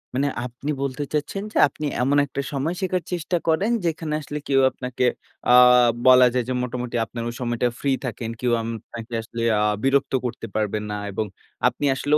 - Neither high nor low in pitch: No, low, 130 Hz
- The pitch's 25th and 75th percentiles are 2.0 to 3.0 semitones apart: No, average, 3.8 semitones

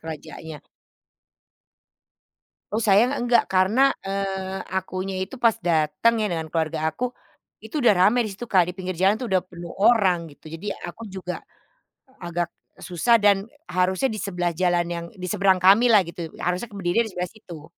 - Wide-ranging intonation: No, average, 3.7 semitones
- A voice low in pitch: No, high, 190 Hz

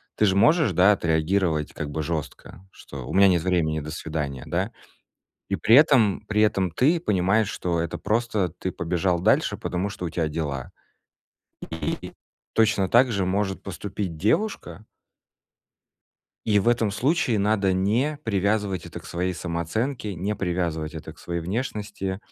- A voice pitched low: Yes, very low, 95 Hz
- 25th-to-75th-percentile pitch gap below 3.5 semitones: No, average, 4.1 semitones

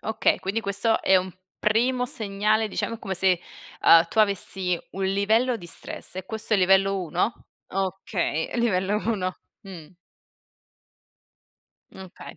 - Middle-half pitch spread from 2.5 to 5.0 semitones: Yes, average, 2.8 semitones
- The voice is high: Yes, high, 195 Hz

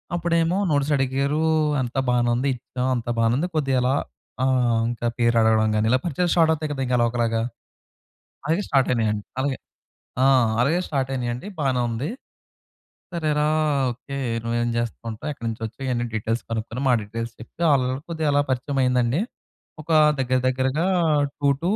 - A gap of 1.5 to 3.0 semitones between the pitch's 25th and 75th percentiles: No, average, 3.4 semitones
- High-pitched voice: No, low, 130 Hz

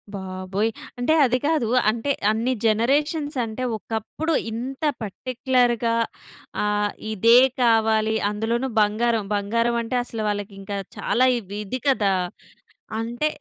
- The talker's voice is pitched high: Yes, high, 230 Hz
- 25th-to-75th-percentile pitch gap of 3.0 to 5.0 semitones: Yes, average, 3.3 semitones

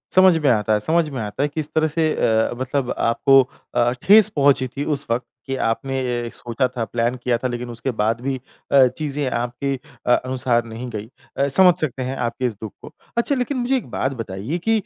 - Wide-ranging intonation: No, average, 3.5 semitones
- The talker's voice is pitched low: Yes, low, 130 Hz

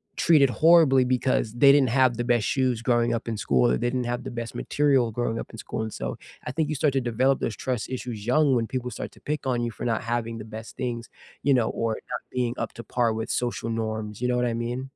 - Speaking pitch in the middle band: No, low, 120 Hz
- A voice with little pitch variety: Yes, narrow, 2.2 semitones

